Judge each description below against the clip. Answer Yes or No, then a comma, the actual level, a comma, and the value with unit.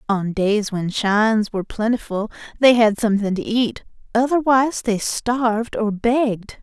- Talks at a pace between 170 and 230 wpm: No, average, 145 wpm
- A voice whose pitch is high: Yes, high, 220 Hz